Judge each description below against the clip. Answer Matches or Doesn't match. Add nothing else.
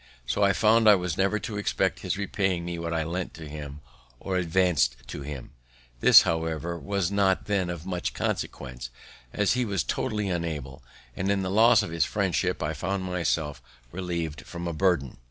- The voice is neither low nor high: Doesn't match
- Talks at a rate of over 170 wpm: Matches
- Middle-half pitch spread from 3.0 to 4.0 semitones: Matches